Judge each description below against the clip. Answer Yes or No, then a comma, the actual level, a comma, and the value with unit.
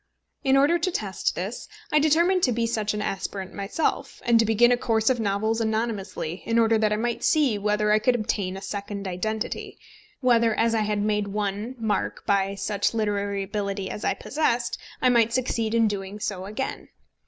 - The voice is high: Yes, high, 215 Hz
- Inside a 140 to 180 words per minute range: No, average, 190 wpm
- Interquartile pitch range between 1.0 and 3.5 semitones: Yes, narrow, 2.6 semitones